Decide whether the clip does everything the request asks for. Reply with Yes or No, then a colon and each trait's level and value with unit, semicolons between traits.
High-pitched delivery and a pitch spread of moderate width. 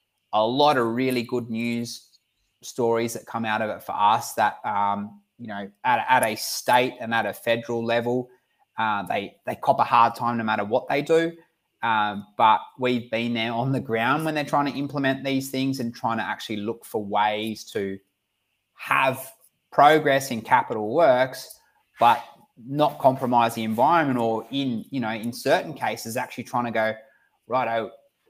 No: low, 120 Hz; average, 3.0 semitones